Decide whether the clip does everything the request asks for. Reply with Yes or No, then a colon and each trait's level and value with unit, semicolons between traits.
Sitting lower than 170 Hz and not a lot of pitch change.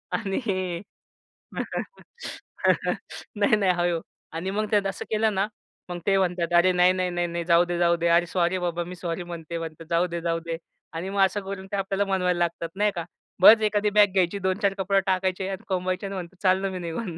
No: medium, 185 Hz; narrow, 2.2 semitones